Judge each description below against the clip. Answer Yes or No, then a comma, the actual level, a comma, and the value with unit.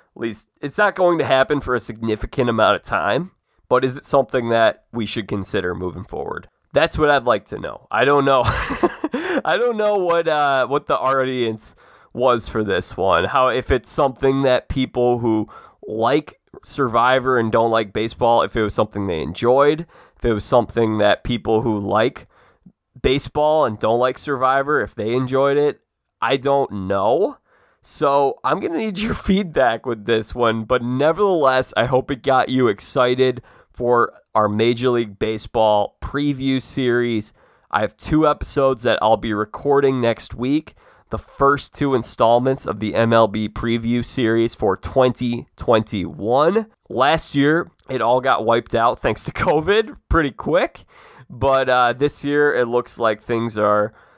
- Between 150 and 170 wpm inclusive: Yes, average, 165 wpm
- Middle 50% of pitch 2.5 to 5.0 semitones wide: Yes, average, 3.8 semitones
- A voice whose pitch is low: Yes, low, 125 Hz